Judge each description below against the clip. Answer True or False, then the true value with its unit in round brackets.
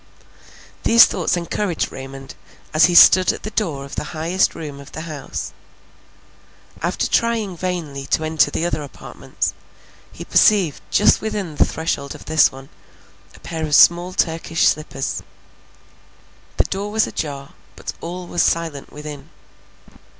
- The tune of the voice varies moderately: True (3.9 semitones)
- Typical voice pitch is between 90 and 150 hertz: False (160 Hz)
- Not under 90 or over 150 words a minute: True (145 wpm)